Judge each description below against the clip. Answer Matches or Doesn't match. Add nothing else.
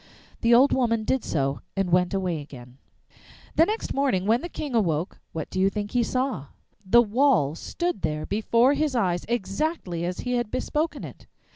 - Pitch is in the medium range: Doesn't match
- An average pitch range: Doesn't match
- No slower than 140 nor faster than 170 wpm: Doesn't match